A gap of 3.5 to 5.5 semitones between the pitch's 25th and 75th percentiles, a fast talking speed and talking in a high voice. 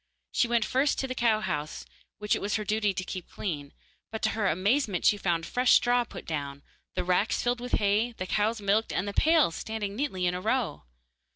Yes: average, 4.6 semitones; fast, 215 wpm; high, 210 Hz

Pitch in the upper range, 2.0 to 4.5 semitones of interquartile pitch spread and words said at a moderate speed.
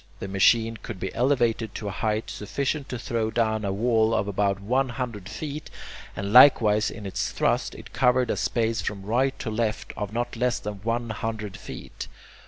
No: low, 115 Hz; average, 2.7 semitones; average, 190 wpm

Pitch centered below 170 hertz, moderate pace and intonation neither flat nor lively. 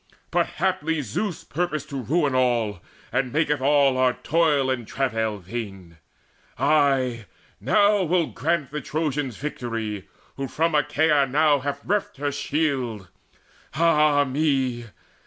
No: medium, 140 Hz; slow, 125 wpm; average, 3.9 semitones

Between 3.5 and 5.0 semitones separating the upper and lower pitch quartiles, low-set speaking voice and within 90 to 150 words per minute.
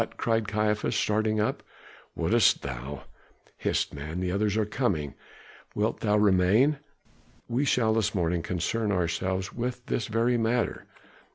Yes: average, 3.8 semitones; low, 105 Hz; average, 140 wpm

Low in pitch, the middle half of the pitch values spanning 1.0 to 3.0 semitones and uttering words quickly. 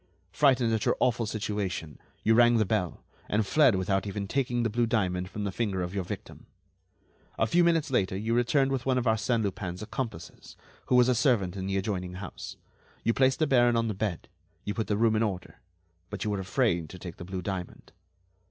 No: low, 110 Hz; average, 4.1 semitones; fast, 210 wpm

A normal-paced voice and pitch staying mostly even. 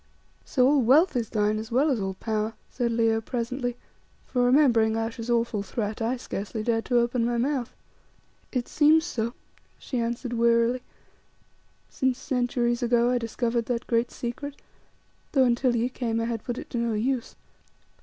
Yes: average, 165 wpm; narrow, 1.7 semitones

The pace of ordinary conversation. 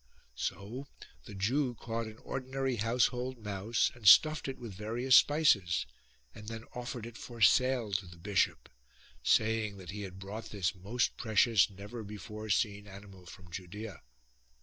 Yes: average, 150 wpm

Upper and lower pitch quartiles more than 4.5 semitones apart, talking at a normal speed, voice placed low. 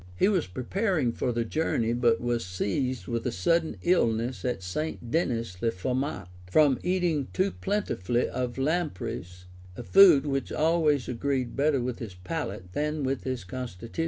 Yes: average, 5.2 semitones; average, 155 wpm; low, 130 Hz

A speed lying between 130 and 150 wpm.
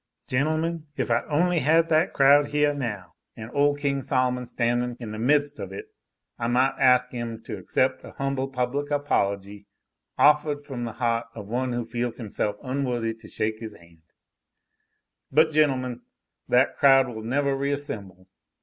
No: average, 165 wpm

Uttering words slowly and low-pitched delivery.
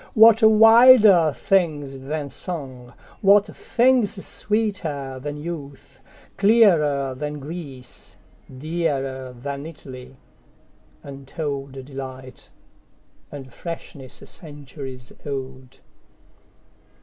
No: slow, 65 wpm; medium, 145 Hz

